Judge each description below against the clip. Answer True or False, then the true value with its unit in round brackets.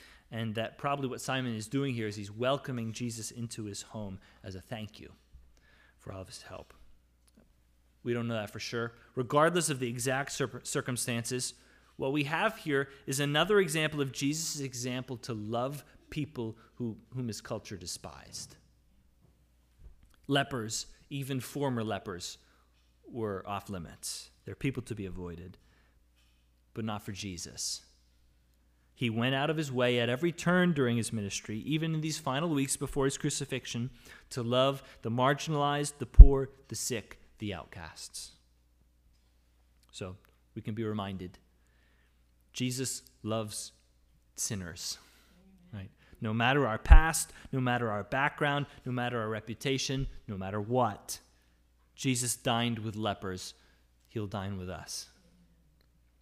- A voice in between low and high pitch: False (115 Hz)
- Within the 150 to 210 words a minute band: False (140 wpm)